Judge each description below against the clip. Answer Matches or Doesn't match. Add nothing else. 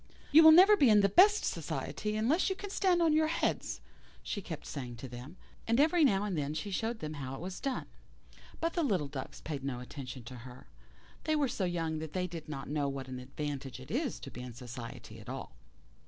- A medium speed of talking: Doesn't match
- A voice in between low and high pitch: Matches